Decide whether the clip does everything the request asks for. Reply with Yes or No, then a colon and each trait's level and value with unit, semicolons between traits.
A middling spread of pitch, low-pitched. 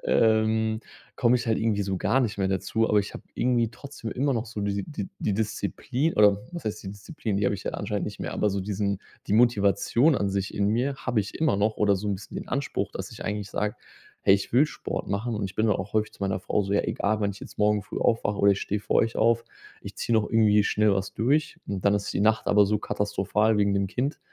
No: narrow, 2.3 semitones; low, 105 Hz